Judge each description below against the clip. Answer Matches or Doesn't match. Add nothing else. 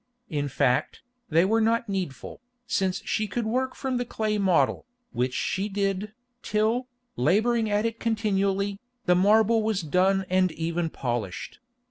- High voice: Matches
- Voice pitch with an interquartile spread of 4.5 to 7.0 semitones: Doesn't match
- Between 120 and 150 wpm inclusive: Matches